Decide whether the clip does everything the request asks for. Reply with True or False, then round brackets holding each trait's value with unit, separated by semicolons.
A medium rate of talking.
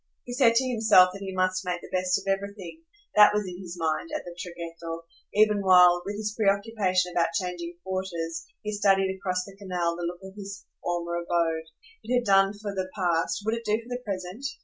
False (210 wpm)